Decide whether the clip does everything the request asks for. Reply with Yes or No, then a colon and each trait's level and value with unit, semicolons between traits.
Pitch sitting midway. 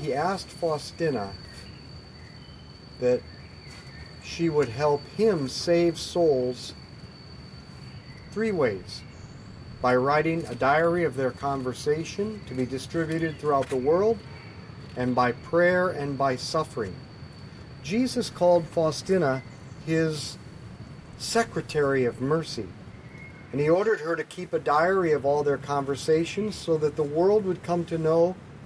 Yes: medium, 150 Hz